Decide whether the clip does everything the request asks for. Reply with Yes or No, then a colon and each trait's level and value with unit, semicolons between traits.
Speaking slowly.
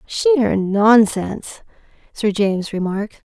Yes: slow, 90 wpm